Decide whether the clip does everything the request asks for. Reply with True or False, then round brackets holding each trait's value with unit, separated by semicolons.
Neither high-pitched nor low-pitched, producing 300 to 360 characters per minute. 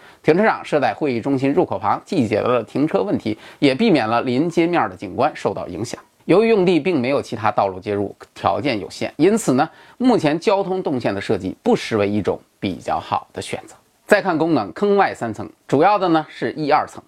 True (150 Hz; 315 characters per minute)